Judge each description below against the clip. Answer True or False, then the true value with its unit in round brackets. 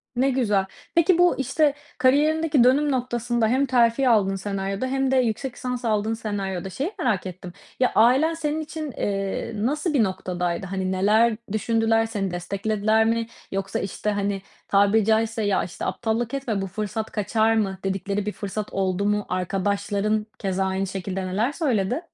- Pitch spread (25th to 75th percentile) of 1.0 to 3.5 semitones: False (4.4 semitones)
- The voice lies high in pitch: True (220 Hz)